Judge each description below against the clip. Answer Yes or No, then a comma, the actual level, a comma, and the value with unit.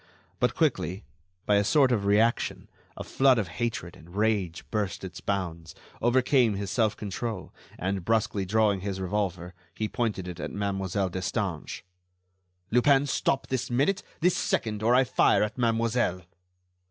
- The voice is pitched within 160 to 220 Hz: No, low, 105 Hz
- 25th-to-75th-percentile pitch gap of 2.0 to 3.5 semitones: No, average, 4.0 semitones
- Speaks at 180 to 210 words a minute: No, average, 150 wpm